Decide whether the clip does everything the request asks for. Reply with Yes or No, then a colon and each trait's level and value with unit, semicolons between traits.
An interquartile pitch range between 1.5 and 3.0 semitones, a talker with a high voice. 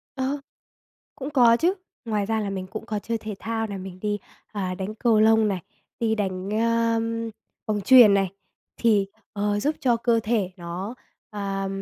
Yes: narrow, 2.6 semitones; high, 215 Hz